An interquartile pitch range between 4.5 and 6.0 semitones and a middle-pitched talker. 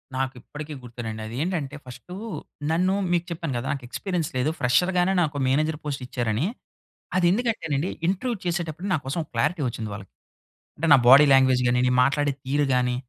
Yes: average, 5.2 semitones; medium, 145 Hz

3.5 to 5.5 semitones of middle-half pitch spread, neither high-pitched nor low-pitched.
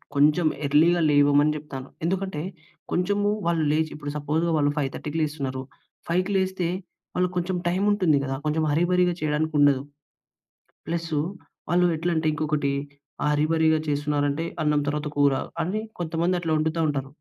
No: average, 3.0 semitones; medium, 155 Hz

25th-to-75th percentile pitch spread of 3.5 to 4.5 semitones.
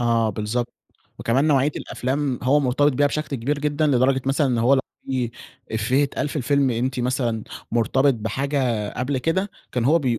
No: average, 3.1 semitones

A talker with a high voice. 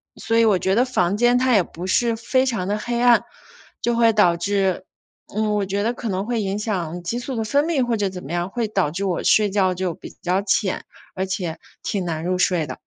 Yes: high, 200 Hz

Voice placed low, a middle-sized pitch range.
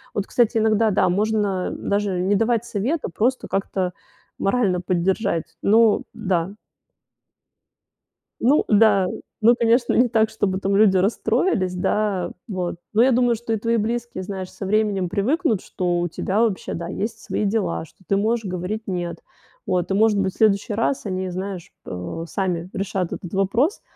No: high, 200 Hz; average, 3.3 semitones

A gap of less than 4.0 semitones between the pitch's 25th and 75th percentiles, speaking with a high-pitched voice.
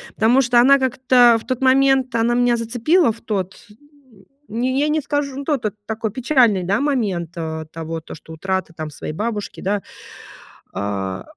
No: wide, 5.6 semitones; high, 230 Hz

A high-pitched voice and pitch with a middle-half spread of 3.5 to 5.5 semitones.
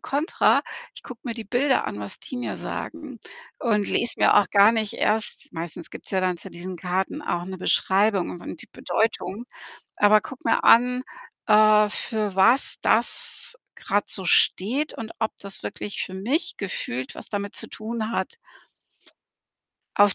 Yes: high, 210 Hz; average, 3.9 semitones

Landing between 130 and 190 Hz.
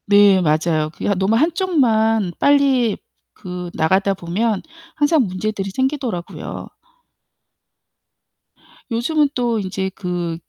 No: high, 205 Hz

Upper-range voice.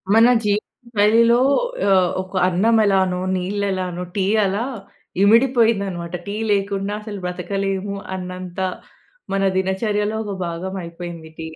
Yes: high, 195 Hz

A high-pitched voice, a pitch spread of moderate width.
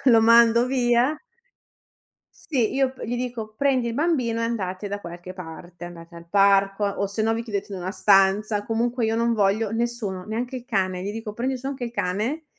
Yes: high, 225 Hz; average, 3.5 semitones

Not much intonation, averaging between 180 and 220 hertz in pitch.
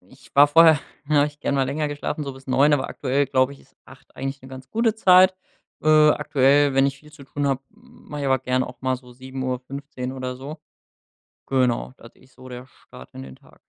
No: narrow, 2.3 semitones; low, 135 Hz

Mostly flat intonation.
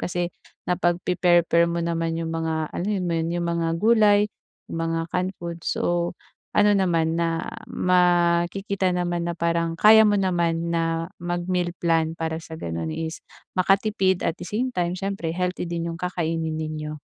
Yes: narrow, 1.7 semitones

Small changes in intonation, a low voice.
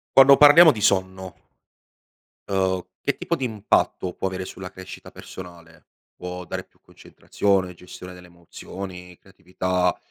Yes: narrow, 1.4 semitones; very low, 95 Hz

